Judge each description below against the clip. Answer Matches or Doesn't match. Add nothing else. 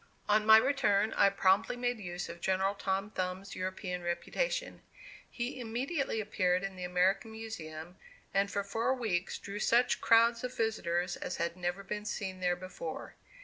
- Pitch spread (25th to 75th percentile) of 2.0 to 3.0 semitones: Doesn't match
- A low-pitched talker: Doesn't match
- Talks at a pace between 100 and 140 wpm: Doesn't match